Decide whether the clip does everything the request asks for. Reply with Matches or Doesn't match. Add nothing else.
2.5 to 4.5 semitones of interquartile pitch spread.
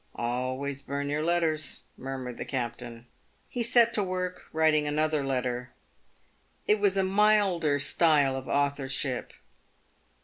Doesn't match